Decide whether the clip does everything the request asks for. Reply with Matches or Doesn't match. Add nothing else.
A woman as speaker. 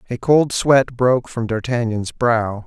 Doesn't match